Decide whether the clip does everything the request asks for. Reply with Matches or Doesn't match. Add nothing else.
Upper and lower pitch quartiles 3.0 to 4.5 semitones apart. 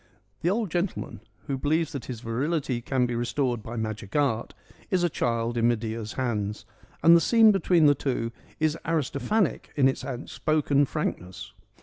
Doesn't match